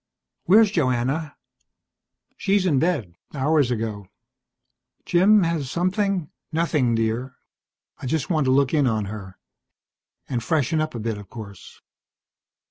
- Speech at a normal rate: No, slow, 130 wpm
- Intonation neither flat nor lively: No, wide, 6.5 semitones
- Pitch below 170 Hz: Yes, medium, 140 Hz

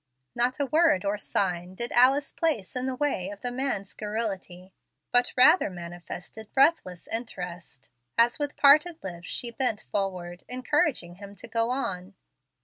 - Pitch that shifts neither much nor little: No, wide, 6.1 semitones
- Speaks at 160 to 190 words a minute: No, average, 150 wpm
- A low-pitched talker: No, high, 225 Hz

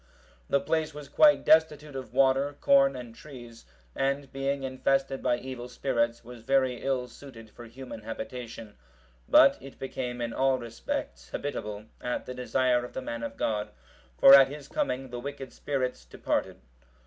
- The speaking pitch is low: Yes, low, 130 Hz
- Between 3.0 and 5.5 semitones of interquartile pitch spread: No, narrow, 2.4 semitones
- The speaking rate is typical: Yes, average, 160 wpm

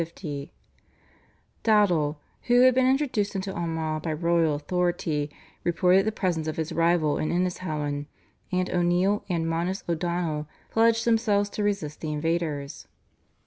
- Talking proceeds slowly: Yes, slow, 130 wpm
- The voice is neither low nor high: Yes, medium, 175 Hz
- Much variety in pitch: No, average, 4.2 semitones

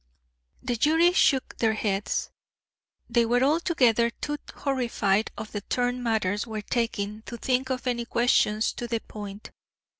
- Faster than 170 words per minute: No, average, 145 wpm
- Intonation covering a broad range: No, average, 2.8 semitones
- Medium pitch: No, high, 235 Hz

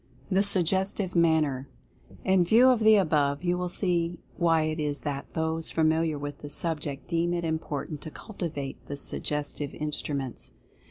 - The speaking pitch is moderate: Yes, medium, 160 Hz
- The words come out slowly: No, average, 155 wpm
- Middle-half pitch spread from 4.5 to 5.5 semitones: No, average, 3.3 semitones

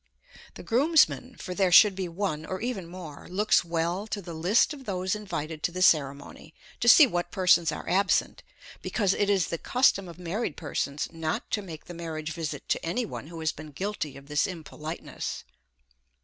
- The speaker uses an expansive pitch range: No, average, 4.0 semitones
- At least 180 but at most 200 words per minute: Yes, average, 190 wpm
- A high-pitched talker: No, medium, 175 Hz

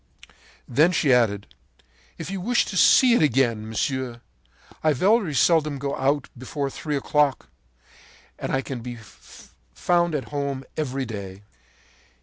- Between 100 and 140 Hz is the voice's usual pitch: Yes, low, 135 Hz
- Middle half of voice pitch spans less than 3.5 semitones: No, average, 4.3 semitones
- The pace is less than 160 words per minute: Yes, slow, 135 wpm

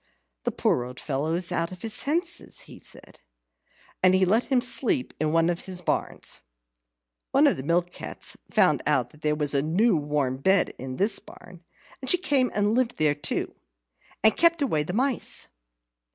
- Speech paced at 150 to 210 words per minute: Yes, average, 185 wpm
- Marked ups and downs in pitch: Yes, wide, 7.4 semitones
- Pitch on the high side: No, medium, 180 Hz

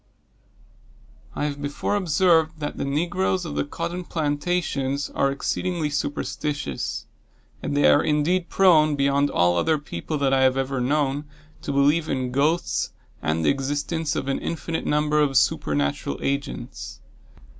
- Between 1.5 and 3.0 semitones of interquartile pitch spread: Yes, average, 2.7 semitones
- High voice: No, medium, 145 Hz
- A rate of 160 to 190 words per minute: No, average, 145 wpm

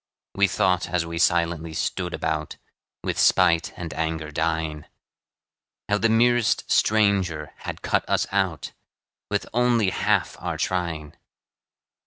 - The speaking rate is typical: No, slow, 125 wpm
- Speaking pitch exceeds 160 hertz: No, very low, 85 Hz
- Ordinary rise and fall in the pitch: Yes, average, 3.8 semitones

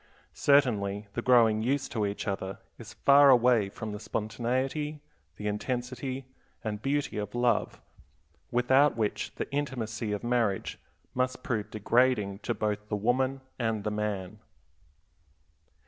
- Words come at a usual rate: No, slow, 130 wpm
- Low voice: Yes, low, 115 Hz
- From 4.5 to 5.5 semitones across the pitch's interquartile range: No, average, 3.5 semitones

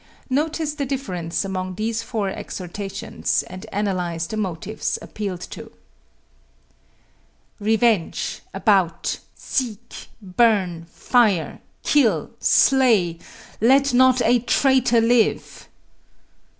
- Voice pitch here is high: Yes, high, 215 Hz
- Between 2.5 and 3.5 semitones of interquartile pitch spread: No, average, 4.9 semitones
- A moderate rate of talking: No, slow, 90 wpm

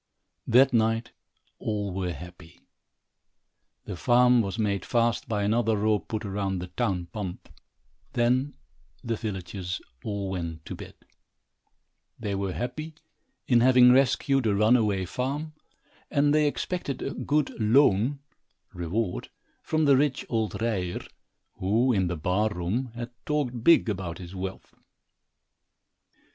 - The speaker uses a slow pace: Yes, slow, 130 wpm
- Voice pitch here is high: No, low, 110 Hz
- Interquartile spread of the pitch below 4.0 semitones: No, average, 4.7 semitones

